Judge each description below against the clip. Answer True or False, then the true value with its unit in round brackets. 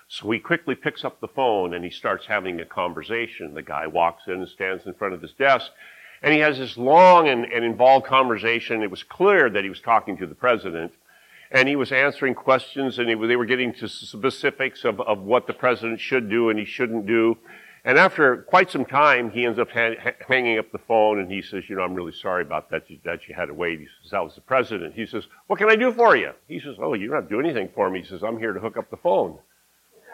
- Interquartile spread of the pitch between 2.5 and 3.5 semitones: True (2.8 semitones)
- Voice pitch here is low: True (120 Hz)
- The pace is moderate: False (255 wpm)